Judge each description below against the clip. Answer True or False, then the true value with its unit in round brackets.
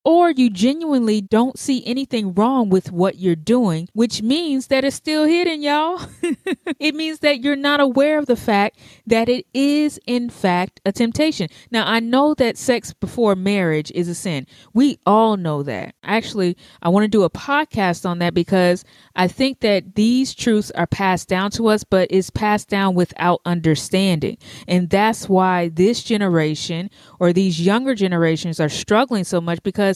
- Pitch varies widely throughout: True (6.1 semitones)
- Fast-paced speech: False (175 wpm)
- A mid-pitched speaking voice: False (205 Hz)